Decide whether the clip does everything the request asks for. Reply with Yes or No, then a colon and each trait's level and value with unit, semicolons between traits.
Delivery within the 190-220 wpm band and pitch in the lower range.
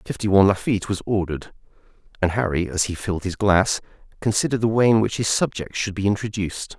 Yes: fast, 205 wpm; low, 100 Hz